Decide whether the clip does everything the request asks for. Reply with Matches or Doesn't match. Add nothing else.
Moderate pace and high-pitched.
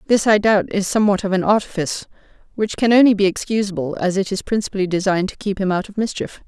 Doesn't match